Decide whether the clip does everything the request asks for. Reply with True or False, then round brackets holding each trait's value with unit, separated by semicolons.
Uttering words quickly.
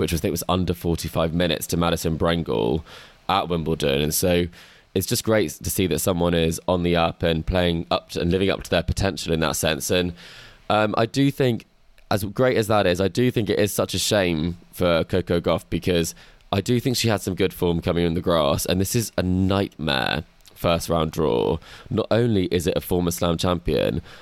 True (225 wpm)